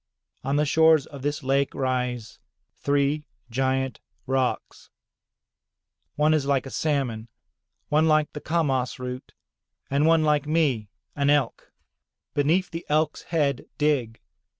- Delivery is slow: Yes, slow, 125 wpm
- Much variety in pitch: No, narrow, 2.6 semitones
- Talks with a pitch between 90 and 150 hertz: Yes, medium, 140 Hz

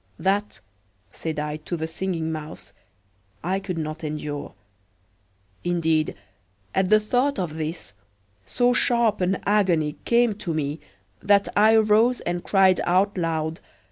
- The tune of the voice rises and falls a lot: No, average, 4.6 semitones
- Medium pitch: Yes, medium, 180 Hz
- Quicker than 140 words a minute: No, slow, 135 wpm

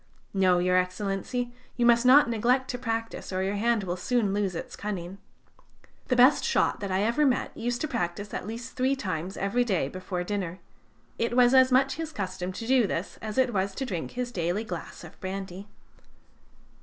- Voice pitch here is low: No, high, 210 Hz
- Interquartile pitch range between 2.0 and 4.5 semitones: No, average, 4.9 semitones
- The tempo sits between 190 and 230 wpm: Yes, average, 195 wpm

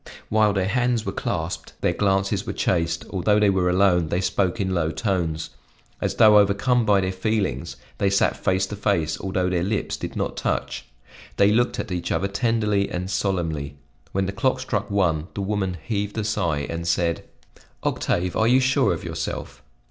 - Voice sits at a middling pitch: No, very low, 95 Hz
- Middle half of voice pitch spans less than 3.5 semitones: Yes, average, 3.0 semitones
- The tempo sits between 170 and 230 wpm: Yes, average, 185 wpm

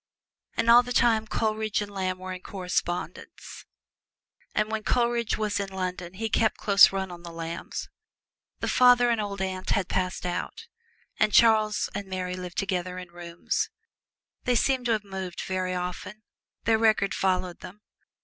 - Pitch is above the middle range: Yes, high, 195 Hz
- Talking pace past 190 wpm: No, average, 165 wpm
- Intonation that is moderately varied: Yes, average, 3.1 semitones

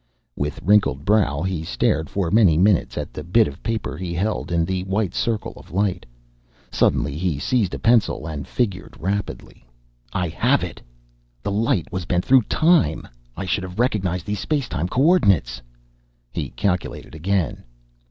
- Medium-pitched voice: No, very low, 95 Hz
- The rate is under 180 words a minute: Yes, average, 160 wpm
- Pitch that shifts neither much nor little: Yes, average, 4.3 semitones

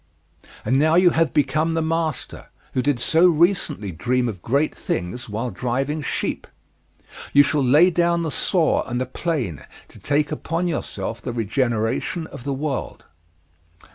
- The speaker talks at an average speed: Yes, average, 155 wpm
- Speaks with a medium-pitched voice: Yes, medium, 145 Hz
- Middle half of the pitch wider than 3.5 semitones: Yes, average, 4.9 semitones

